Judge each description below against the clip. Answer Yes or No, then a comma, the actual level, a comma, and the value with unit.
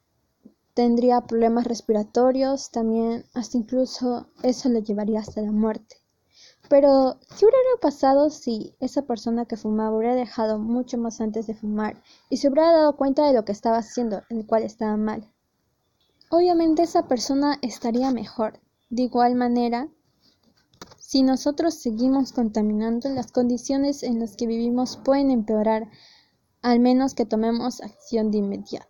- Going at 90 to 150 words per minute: Yes, average, 145 wpm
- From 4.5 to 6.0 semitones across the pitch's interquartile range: No, average, 3.1 semitones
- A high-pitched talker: Yes, high, 245 Hz